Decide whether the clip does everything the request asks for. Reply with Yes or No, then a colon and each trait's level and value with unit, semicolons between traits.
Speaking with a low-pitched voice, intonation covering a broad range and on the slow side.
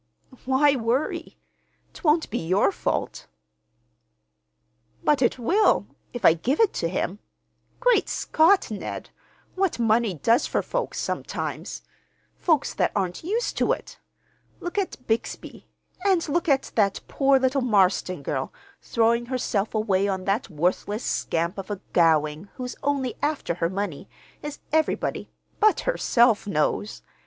No: high, 235 Hz; wide, 7.3 semitones; slow, 130 wpm